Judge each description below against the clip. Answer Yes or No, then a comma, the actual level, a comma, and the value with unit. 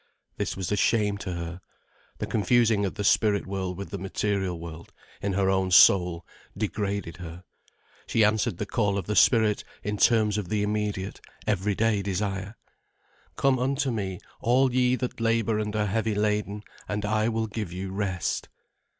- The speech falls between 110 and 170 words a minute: Yes, average, 165 wpm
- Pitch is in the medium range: No, low, 105 Hz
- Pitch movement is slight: Yes, narrow, 2.3 semitones